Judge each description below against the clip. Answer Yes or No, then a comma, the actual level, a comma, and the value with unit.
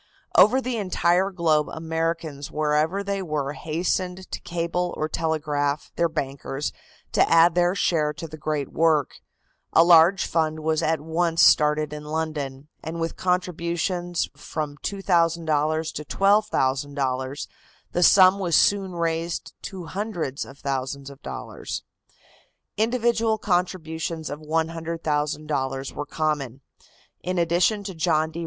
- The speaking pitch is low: No, medium, 160 Hz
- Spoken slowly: Yes, slow, 130 wpm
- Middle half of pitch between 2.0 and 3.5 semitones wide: Yes, average, 2.8 semitones